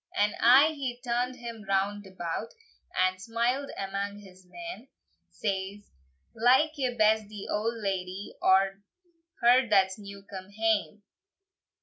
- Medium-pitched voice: No, high, 210 Hz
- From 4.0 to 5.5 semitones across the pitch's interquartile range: No, average, 3.6 semitones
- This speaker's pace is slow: Yes, slow, 125 wpm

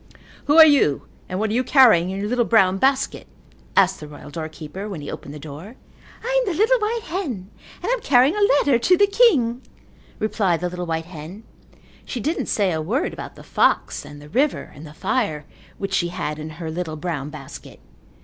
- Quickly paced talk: Yes, fast, 210 wpm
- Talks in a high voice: Yes, high, 200 Hz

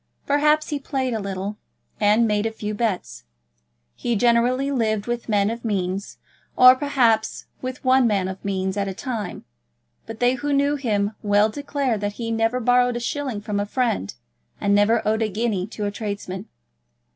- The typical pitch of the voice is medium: No, high, 225 Hz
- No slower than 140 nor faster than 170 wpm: No, average, 180 wpm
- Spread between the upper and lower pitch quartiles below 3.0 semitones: No, average, 3.6 semitones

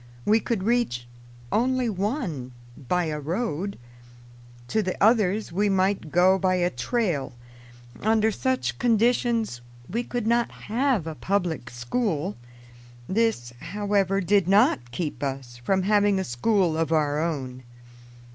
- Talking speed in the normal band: No, slow, 130 wpm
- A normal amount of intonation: No, wide, 6.1 semitones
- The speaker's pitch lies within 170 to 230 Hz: Yes, high, 190 Hz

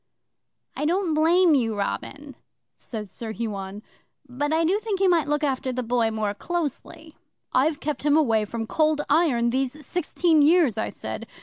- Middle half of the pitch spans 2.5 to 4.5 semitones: No, wide, 5.5 semitones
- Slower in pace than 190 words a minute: Yes, average, 170 wpm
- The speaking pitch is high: Yes, very high, 290 Hz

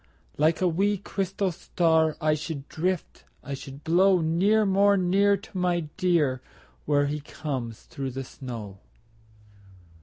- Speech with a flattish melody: No, average, 4.8 semitones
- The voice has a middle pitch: Yes, medium, 165 Hz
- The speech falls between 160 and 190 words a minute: No, average, 140 wpm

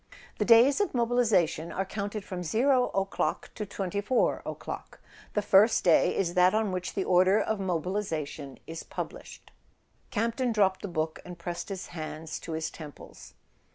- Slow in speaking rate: No, average, 155 wpm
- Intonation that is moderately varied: Yes, average, 4.1 semitones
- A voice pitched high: Yes, high, 195 Hz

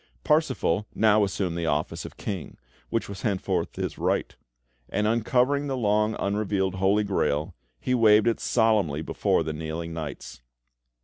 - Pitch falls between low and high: No, low, 105 Hz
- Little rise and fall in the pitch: No, average, 4.9 semitones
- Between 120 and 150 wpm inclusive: Yes, average, 145 wpm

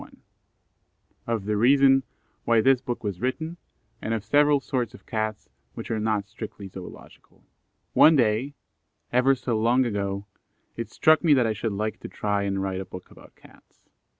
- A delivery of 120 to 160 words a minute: No, average, 175 wpm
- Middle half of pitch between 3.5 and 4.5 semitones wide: Yes, average, 4.2 semitones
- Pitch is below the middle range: Yes, low, 115 Hz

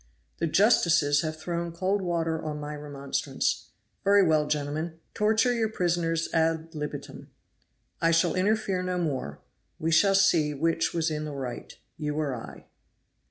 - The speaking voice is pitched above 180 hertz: No, medium, 165 Hz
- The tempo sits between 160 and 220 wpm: No, average, 150 wpm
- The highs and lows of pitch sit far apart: No, average, 3.2 semitones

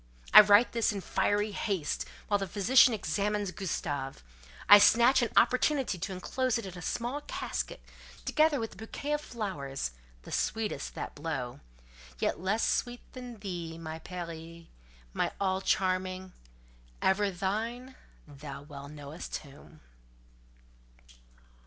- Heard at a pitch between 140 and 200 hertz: Yes, high, 190 Hz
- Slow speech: Yes, slow, 125 wpm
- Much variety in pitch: Yes, wide, 6.5 semitones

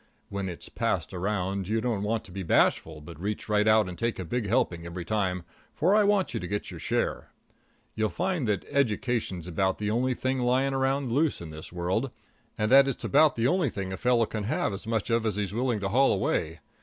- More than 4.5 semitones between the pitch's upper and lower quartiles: Yes, average, 5.0 semitones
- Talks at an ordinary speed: No, fast, 225 wpm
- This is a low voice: Yes, low, 110 Hz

